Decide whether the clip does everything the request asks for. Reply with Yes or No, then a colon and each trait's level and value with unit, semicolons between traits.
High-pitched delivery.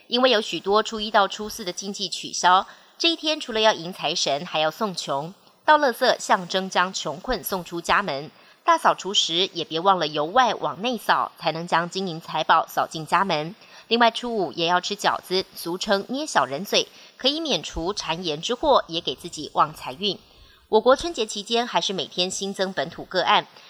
Yes: high, 195 Hz